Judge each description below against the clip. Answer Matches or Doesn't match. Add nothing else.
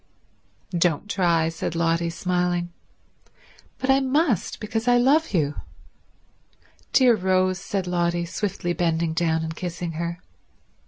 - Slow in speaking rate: Matches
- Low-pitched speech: Doesn't match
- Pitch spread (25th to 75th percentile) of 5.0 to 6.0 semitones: Doesn't match